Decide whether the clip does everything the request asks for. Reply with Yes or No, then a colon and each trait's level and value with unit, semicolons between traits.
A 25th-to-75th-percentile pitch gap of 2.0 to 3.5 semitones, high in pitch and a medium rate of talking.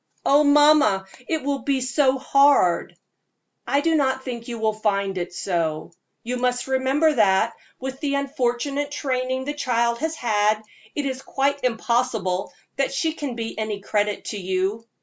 No: average, 4.5 semitones; very high, 255 Hz; average, 160 wpm